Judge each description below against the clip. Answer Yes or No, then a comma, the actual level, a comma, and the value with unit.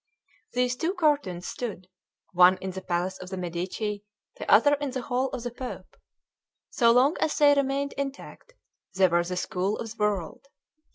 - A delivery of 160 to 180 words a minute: Yes, average, 175 wpm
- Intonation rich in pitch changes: Yes, wide, 6.7 semitones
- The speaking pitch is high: Yes, high, 225 Hz